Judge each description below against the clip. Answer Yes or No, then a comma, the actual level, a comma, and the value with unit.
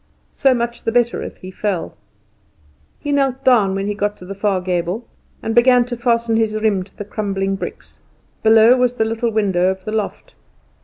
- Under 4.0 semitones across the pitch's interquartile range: Yes, average, 3.5 semitones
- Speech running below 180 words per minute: No, average, 195 wpm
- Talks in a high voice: Yes, high, 220 Hz